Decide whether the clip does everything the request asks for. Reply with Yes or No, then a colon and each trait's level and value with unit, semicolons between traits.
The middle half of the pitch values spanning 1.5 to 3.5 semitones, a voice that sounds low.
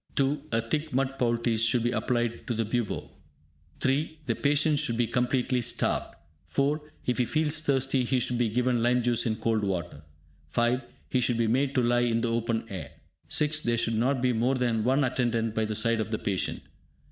Yes: narrow, 2.6 semitones; low, 120 Hz